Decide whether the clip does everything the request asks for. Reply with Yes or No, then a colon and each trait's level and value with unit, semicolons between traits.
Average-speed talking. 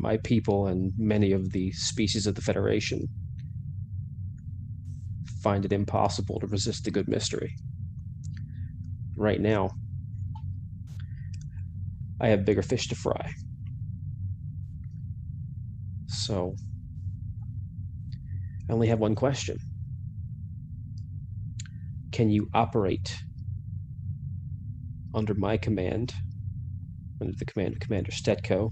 No: slow, 90 wpm